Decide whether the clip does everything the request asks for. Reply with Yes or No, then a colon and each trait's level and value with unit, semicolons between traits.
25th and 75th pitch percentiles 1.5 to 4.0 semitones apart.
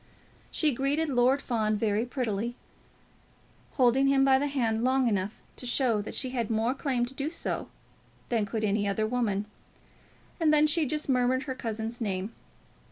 Yes: average, 3.5 semitones